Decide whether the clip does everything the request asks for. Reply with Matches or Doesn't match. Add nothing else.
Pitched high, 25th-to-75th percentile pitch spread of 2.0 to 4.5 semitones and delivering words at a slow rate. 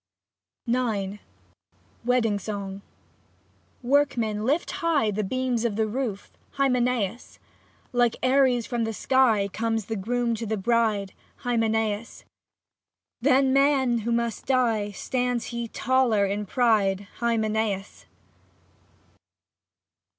Matches